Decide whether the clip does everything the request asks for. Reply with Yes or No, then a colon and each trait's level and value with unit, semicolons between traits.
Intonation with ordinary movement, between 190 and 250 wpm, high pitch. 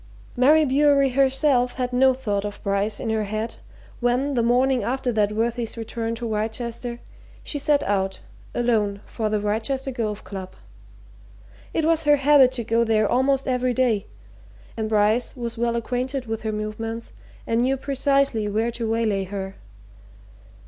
No: average, 3.4 semitones; average, 155 wpm; high, 235 Hz